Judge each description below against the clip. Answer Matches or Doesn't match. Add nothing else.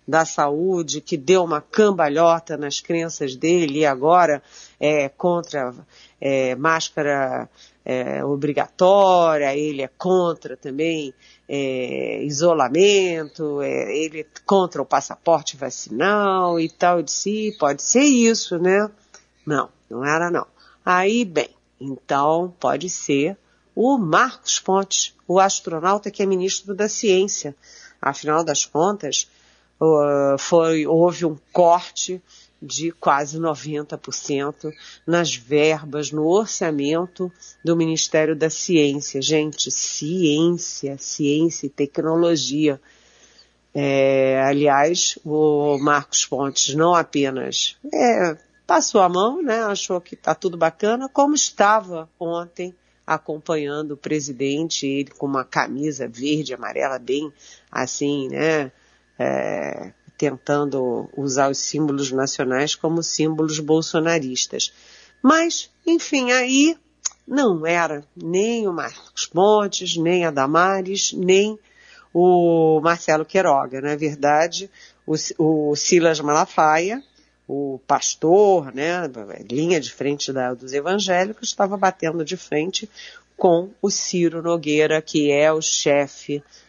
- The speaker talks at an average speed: Doesn't match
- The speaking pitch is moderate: Matches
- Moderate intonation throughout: Matches